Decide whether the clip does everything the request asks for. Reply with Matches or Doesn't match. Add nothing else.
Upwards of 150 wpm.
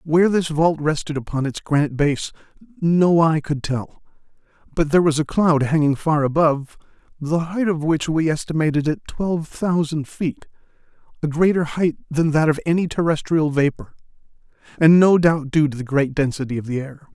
Matches